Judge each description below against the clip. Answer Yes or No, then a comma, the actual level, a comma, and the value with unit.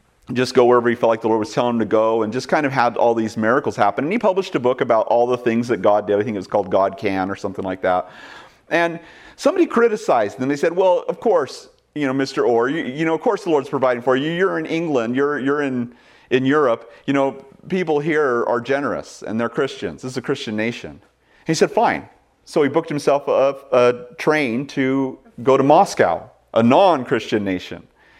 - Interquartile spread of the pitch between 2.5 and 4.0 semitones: No, average, 4.6 semitones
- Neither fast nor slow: No, fast, 230 wpm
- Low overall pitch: Yes, low, 130 Hz